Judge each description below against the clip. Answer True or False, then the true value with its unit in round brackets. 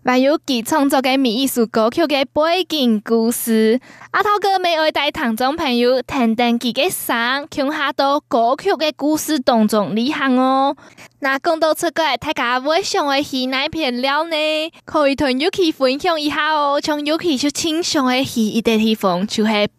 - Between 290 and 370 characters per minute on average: False (260 characters per minute)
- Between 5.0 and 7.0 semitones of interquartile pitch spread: False (4.1 semitones)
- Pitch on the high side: True (280 Hz)